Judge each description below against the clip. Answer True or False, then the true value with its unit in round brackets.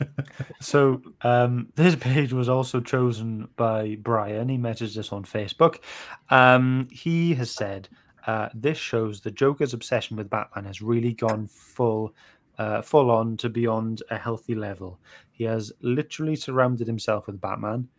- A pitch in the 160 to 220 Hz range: False (115 Hz)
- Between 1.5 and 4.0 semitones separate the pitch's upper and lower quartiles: True (3.0 semitones)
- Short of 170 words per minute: True (150 wpm)